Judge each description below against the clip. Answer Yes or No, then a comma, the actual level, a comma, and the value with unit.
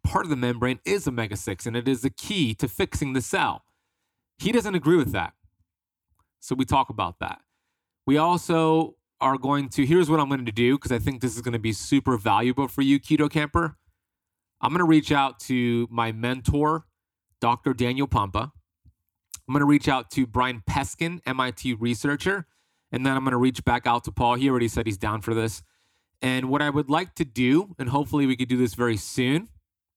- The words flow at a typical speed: No, fast, 210 wpm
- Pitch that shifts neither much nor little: Yes, average, 3.9 semitones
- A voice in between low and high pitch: No, low, 130 Hz